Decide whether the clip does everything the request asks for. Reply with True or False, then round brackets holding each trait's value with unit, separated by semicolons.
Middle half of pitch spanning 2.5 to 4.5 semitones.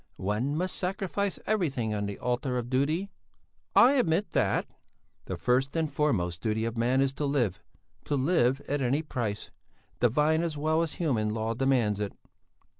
False (5.6 semitones)